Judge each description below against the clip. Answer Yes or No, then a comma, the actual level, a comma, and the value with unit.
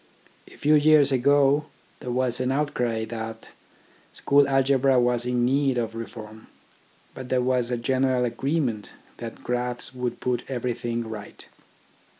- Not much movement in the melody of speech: Yes, narrow, 2.2 semitones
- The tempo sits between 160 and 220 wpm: No, average, 140 wpm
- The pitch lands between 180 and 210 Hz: No, low, 125 Hz